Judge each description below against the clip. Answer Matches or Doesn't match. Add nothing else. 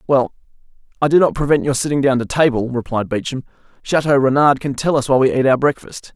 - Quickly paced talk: Matches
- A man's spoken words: Matches